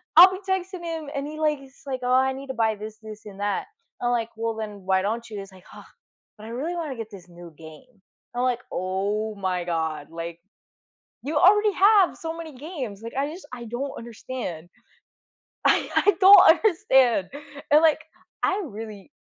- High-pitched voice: Yes, high, 240 Hz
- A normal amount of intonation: No, wide, 7.3 semitones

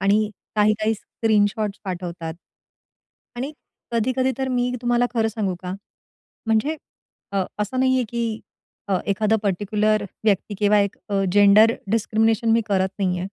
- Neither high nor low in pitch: No, high, 215 Hz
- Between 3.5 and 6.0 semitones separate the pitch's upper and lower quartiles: No, narrow, 2.5 semitones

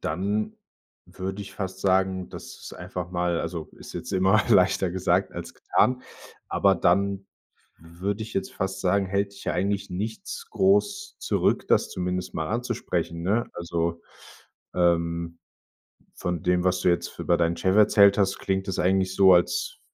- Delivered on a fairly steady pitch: Yes, narrow, 2.3 semitones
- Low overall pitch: Yes, very low, 95 Hz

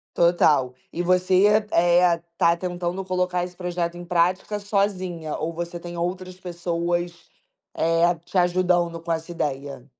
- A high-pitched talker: No, medium, 175 Hz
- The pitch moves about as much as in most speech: No, narrow, 1.3 semitones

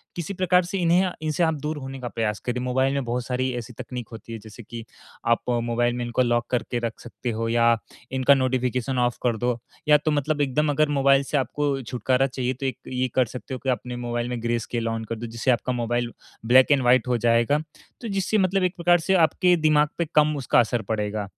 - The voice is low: Yes, low, 125 Hz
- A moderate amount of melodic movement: Yes, average, 3.6 semitones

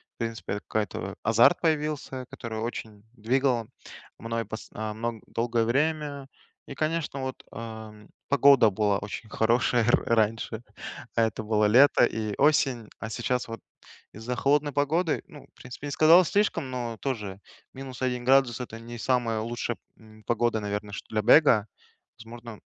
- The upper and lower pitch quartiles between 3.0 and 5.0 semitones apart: Yes, average, 3.5 semitones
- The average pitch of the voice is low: Yes, low, 120 Hz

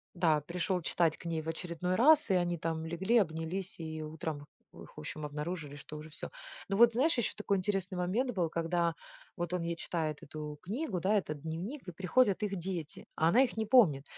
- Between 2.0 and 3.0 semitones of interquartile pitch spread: No, average, 3.7 semitones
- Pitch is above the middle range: No, medium, 175 Hz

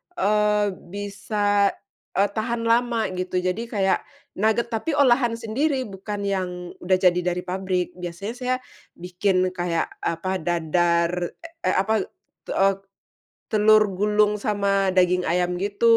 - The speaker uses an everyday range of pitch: Yes, average, 3.2 semitones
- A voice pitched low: No, high, 200 Hz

